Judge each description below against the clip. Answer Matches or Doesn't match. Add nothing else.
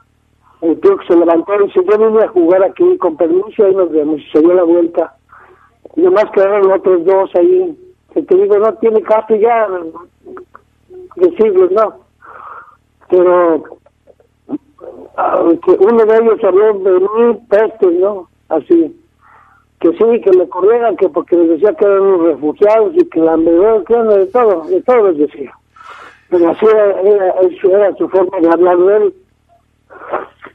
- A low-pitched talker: Doesn't match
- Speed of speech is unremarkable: Matches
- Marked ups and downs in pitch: Matches